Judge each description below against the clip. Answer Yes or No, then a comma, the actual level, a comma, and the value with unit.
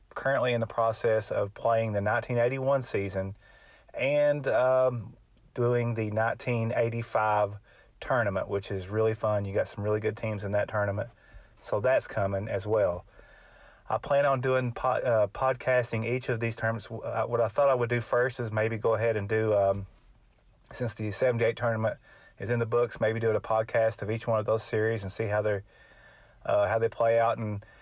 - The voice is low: Yes, low, 115 Hz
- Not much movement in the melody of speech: Yes, narrow, 2.1 semitones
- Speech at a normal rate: Yes, average, 185 wpm